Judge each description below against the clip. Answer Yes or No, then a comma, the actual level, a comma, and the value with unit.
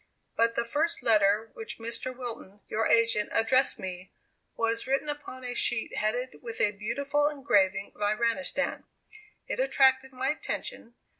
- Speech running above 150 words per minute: No, average, 145 wpm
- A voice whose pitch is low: No, high, 235 Hz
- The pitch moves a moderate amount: Yes, average, 3.5 semitones